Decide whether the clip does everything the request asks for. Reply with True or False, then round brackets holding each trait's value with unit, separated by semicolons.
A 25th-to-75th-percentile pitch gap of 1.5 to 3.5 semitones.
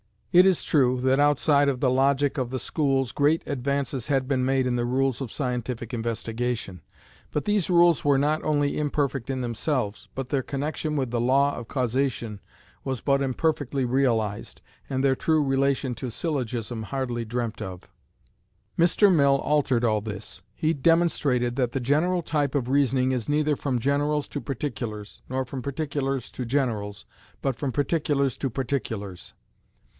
True (2.9 semitones)